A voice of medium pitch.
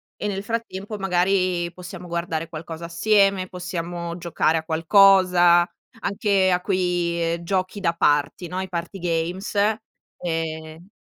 Yes: medium, 175 Hz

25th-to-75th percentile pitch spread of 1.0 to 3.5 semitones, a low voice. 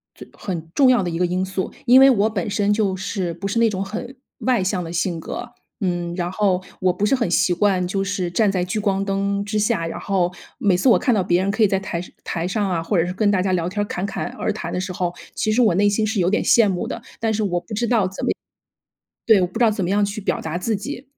No: average, 3.0 semitones; high, 195 Hz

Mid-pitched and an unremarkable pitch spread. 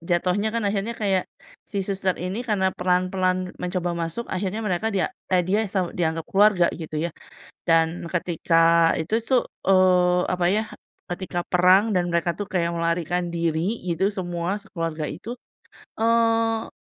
Yes: medium, 180 Hz; average, 3.0 semitones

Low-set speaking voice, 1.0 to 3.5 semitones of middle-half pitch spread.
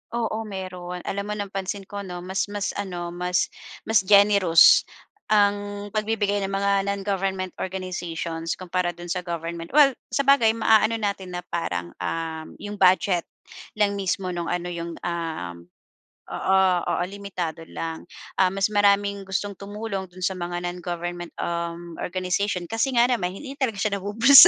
No: high, 190 Hz; average, 2.7 semitones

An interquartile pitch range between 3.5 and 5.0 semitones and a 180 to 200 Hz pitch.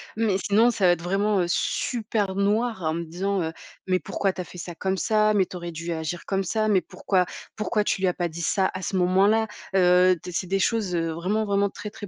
No: average, 2.8 semitones; high, 190 Hz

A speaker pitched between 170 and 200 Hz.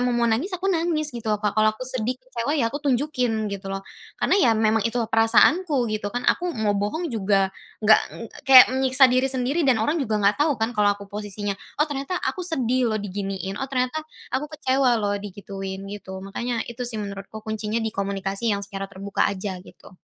No: high, 225 Hz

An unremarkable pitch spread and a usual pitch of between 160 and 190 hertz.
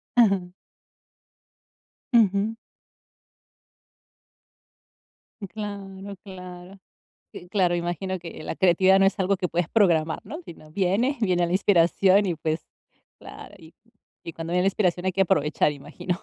No: narrow, 2.3 semitones; medium, 185 Hz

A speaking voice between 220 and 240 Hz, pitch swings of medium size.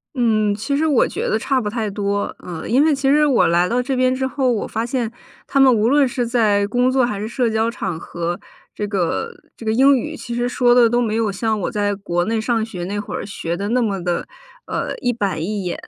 Yes: high, 225 Hz; average, 3.7 semitones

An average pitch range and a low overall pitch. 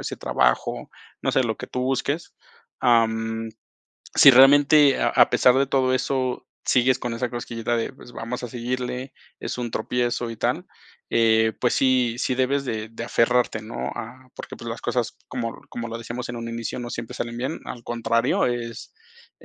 No: narrow, 1.8 semitones; low, 120 Hz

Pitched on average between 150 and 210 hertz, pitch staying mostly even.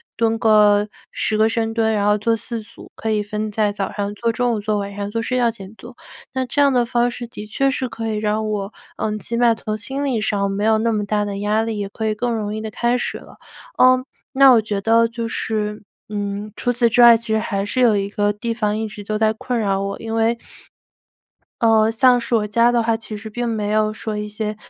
No: high, 220 Hz; narrow, 1.9 semitones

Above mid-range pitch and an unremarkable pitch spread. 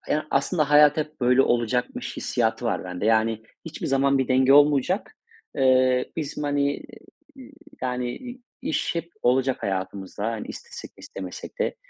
No: low, 135 Hz; average, 3.7 semitones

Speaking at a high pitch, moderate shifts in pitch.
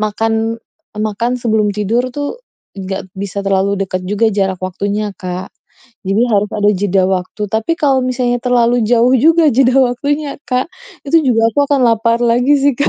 Yes: high, 225 Hz; average, 3.9 semitones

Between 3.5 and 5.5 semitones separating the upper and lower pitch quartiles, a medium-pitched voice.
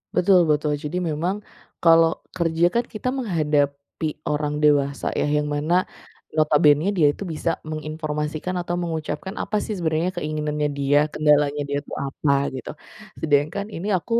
No: narrow, 2.6 semitones; medium, 155 Hz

